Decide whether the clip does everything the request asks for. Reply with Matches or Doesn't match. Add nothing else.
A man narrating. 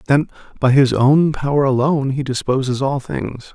Matches